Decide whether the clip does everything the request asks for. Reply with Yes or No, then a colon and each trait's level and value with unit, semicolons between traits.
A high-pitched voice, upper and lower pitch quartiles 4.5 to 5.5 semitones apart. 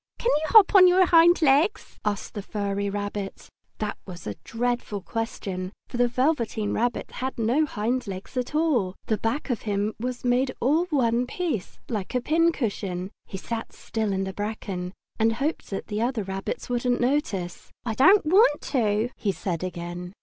Yes: high, 230 Hz; average, 5.1 semitones